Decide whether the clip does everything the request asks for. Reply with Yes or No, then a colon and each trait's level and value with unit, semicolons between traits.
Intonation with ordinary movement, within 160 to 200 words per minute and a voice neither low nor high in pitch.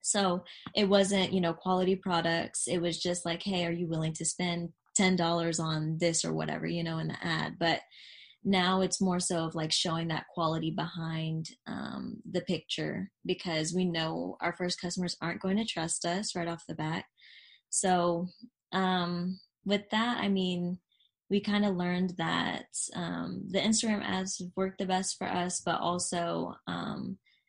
No: narrow, 2.3 semitones; average, 170 wpm; medium, 180 Hz